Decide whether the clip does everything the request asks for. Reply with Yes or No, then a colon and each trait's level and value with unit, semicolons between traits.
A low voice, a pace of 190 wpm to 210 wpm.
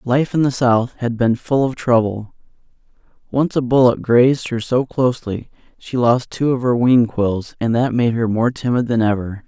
Yes: low, 120 Hz; average, 195 wpm